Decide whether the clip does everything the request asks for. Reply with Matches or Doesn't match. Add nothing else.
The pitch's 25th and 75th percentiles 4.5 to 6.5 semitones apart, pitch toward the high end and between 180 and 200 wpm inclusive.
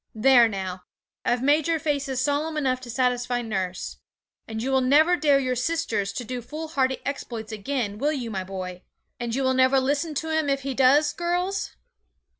Doesn't match